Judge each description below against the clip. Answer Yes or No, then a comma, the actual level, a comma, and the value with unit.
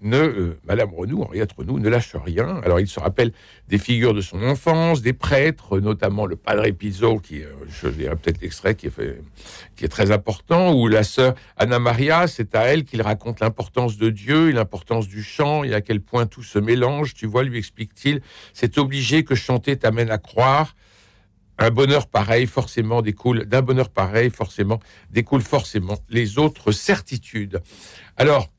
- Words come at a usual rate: Yes, average, 185 wpm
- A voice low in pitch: Yes, low, 115 Hz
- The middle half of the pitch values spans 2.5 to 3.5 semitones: No, average, 4.1 semitones